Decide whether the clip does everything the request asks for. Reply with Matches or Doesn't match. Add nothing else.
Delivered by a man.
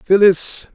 Matches